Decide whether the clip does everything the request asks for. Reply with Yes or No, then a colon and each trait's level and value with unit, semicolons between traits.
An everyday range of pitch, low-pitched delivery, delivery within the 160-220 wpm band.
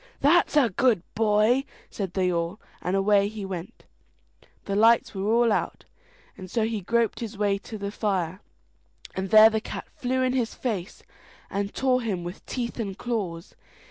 No: average, 3.4 semitones; high, 210 Hz; average, 175 wpm